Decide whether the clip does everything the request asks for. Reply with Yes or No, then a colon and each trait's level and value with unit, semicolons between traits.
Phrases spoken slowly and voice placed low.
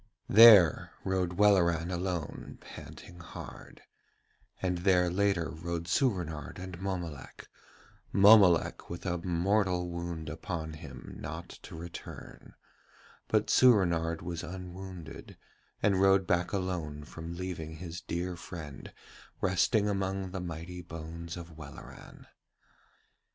Yes: slow, 110 wpm; very low, 90 Hz